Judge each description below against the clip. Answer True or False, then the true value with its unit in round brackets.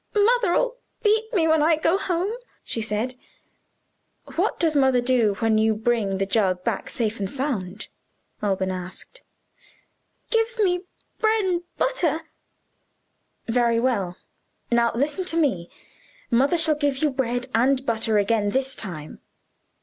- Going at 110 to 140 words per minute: True (135 wpm)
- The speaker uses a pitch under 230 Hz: False (255 Hz)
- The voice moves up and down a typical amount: False (7.5 semitones)